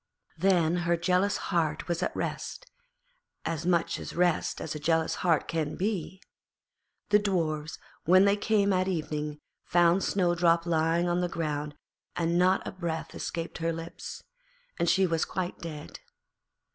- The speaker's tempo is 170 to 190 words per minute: No, average, 150 wpm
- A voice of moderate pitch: Yes, medium, 170 Hz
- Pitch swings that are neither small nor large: No, narrow, 2.2 semitones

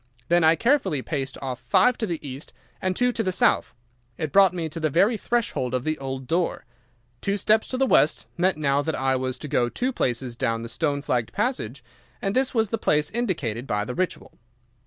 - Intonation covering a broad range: Yes, wide, 7.3 semitones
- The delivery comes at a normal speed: No, fast, 215 wpm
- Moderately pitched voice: Yes, medium, 155 Hz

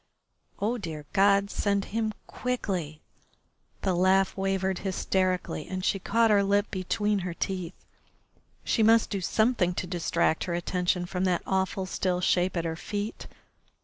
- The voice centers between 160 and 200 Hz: Yes, high, 190 Hz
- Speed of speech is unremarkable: Yes, average, 150 wpm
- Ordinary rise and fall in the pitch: No, narrow, 2.2 semitones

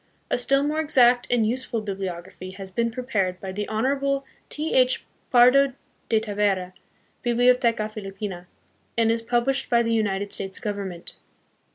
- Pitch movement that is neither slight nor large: Yes, average, 4.2 semitones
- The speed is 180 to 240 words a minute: No, average, 145 wpm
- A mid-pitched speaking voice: No, high, 225 Hz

